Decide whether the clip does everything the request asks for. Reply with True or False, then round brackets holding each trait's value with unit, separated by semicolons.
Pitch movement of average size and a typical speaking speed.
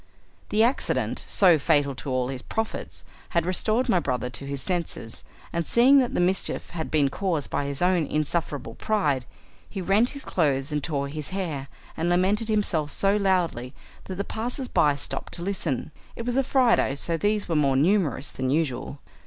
False (6.1 semitones; 185 wpm)